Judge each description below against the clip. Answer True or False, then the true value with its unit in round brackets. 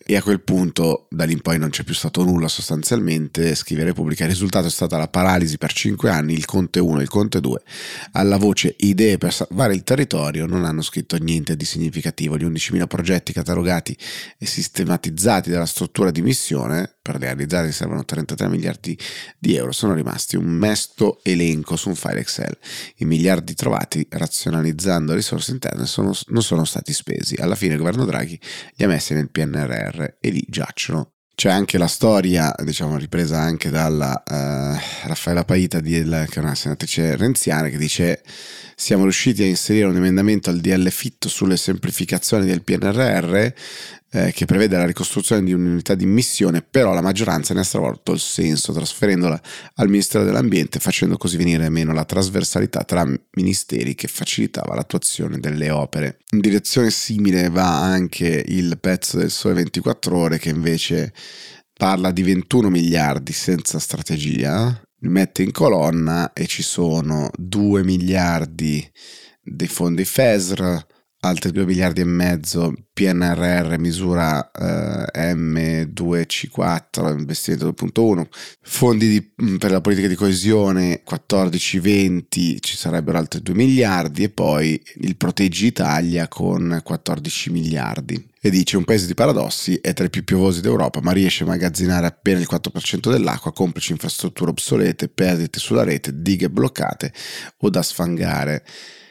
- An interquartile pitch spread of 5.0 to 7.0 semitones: False (2.8 semitones)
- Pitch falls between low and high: False (90 Hz)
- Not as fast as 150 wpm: False (155 wpm)